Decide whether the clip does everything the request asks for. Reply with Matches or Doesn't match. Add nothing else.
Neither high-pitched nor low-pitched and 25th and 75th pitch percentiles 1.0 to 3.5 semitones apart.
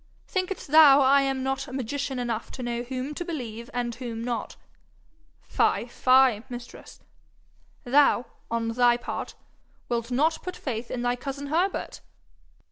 Doesn't match